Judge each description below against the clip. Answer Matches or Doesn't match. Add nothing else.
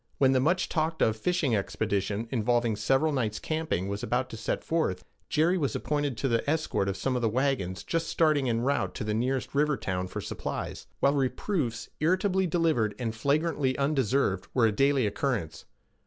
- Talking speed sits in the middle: Matches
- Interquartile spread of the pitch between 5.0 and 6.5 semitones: Matches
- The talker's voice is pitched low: Matches